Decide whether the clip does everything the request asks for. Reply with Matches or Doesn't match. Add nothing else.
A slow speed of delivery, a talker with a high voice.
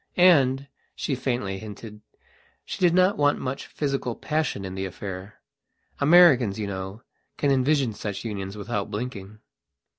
Doesn't match